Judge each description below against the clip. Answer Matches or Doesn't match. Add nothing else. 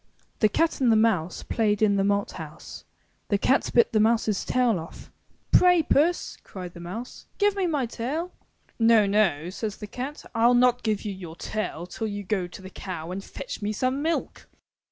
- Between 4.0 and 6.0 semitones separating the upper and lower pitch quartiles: Matches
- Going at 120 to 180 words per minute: Doesn't match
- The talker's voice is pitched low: Doesn't match